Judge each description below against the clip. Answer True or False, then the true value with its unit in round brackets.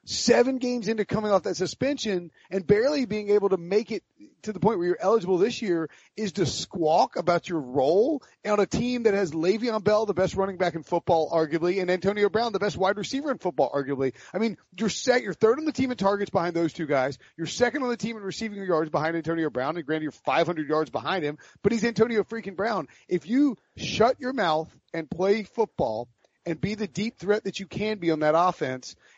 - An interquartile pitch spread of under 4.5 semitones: False (4.8 semitones)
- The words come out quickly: True (225 wpm)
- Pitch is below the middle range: False (195 Hz)